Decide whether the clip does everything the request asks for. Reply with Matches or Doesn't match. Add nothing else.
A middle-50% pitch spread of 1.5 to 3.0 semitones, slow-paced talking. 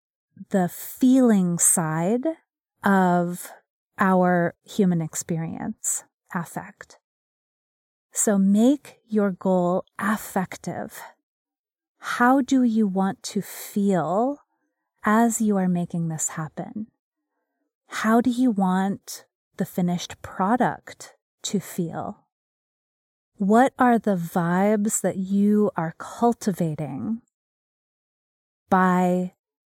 Doesn't match